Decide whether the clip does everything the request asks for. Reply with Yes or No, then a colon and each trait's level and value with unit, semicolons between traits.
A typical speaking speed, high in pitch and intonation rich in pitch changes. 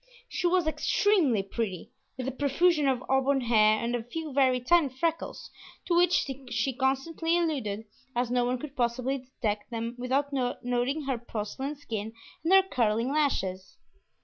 No: average, 155 wpm; very high, 260 Hz; average, 4.1 semitones